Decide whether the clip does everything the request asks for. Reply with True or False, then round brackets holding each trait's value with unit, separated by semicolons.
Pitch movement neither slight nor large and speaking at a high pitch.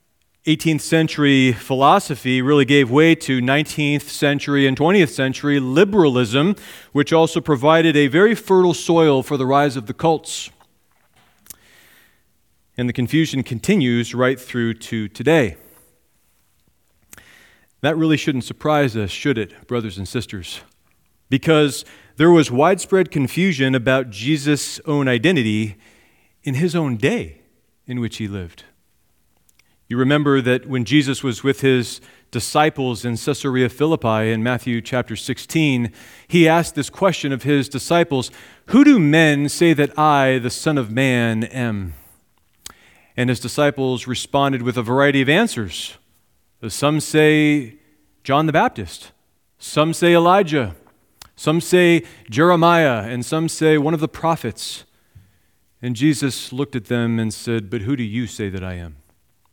False (4.3 semitones; 135 Hz)